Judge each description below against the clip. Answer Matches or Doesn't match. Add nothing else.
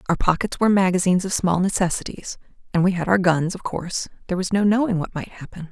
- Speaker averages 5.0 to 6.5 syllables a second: Doesn't match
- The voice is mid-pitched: Matches